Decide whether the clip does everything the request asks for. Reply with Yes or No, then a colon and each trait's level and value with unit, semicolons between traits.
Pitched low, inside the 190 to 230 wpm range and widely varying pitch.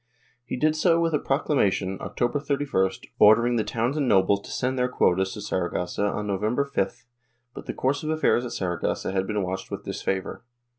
Yes: low, 115 Hz; average, 195 wpm; wide, 6.6 semitones